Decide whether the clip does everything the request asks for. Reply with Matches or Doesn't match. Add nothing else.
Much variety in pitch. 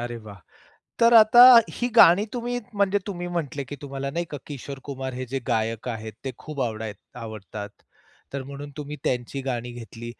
Matches